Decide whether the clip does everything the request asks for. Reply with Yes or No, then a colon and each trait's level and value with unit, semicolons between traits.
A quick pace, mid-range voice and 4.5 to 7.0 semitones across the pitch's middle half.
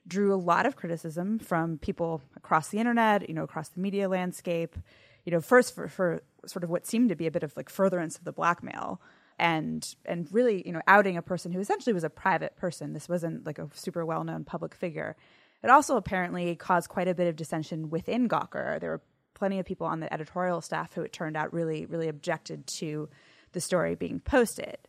No: fast, 215 wpm; medium, 175 Hz; average, 3.0 semitones